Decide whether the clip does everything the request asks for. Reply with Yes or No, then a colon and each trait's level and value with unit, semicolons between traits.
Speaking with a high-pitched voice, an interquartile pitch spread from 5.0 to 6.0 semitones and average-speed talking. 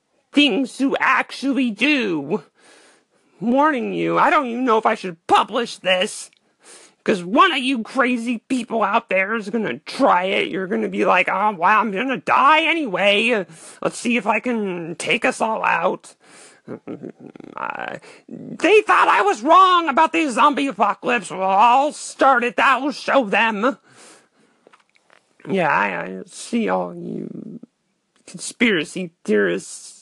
Yes: high, 235 Hz; average, 5.3 semitones; average, 150 wpm